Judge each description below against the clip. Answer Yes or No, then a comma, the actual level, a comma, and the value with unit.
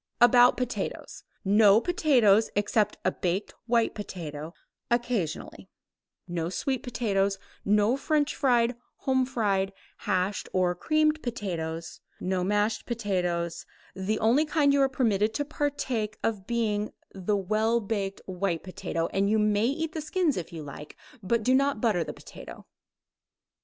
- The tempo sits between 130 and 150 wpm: Yes, average, 140 wpm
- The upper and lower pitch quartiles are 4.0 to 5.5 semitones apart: Yes, average, 4.7 semitones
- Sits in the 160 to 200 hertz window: No, high, 215 Hz